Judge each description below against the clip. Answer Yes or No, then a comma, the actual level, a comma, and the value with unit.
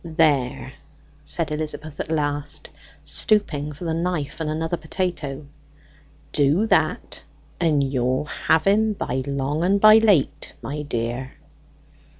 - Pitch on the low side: No, medium, 150 Hz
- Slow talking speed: Yes, slow, 125 wpm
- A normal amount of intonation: Yes, average, 3.6 semitones